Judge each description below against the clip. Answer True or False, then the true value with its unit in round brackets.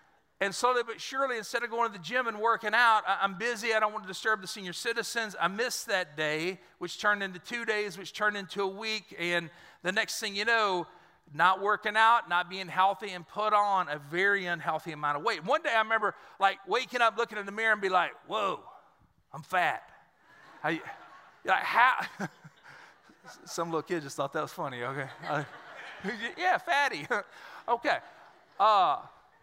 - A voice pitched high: True (205 Hz)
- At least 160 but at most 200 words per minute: True (190 wpm)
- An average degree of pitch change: True (4.1 semitones)